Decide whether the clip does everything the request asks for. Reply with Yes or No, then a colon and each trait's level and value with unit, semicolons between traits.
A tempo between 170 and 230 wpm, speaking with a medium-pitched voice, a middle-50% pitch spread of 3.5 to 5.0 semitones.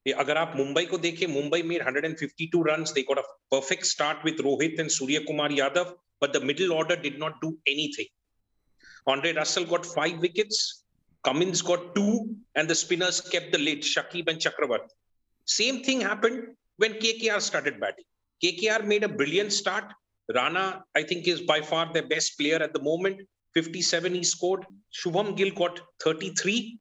Yes: average, 175 wpm; medium, 175 Hz; average, 4.1 semitones